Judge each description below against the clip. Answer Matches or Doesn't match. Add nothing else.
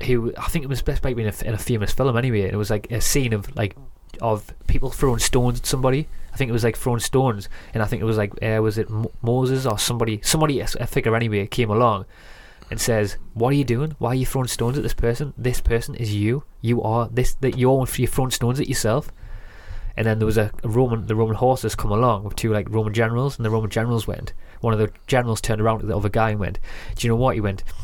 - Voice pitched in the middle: Doesn't match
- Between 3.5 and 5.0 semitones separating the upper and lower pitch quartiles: Doesn't match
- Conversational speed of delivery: Doesn't match